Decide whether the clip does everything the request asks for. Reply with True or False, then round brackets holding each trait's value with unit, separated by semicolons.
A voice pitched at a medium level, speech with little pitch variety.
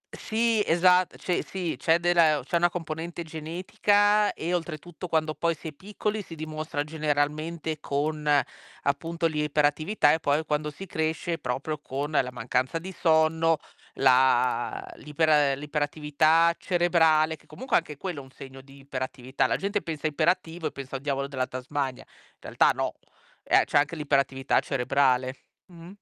False (155 Hz; 3.0 semitones)